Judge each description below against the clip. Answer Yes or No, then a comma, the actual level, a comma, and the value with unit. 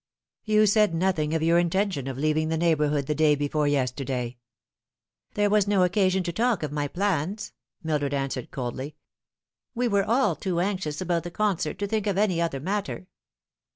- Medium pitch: Yes, medium, 170 Hz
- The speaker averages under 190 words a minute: No, average, 195 wpm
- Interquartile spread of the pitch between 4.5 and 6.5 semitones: Yes, average, 5.3 semitones